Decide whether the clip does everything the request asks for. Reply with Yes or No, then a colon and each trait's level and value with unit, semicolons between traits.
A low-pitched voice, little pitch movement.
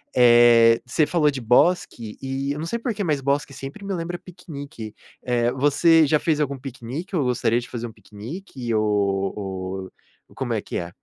No: low, 130 Hz; average, 5.1 semitones